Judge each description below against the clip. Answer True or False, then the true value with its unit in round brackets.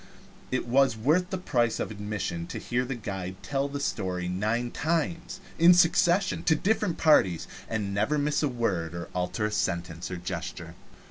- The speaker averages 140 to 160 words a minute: False (180 wpm)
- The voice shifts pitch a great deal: True (8.3 semitones)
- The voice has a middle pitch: False (120 Hz)